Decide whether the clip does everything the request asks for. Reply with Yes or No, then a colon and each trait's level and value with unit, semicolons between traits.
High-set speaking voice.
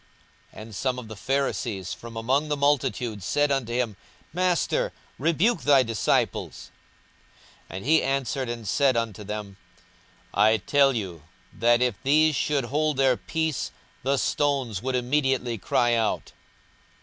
No: low, 125 Hz